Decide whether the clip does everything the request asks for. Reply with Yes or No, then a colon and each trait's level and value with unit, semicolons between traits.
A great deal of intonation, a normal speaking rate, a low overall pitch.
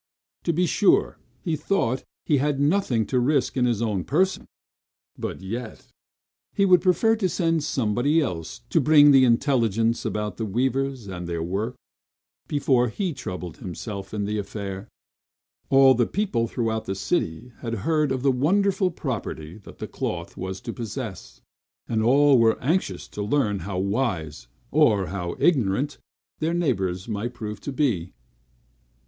Yes: wide, 6.4 semitones; average, 150 wpm; low, 120 Hz